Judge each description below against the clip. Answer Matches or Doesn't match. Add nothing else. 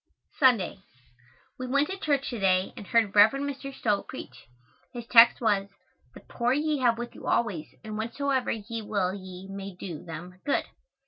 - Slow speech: Doesn't match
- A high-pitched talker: Matches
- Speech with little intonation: Doesn't match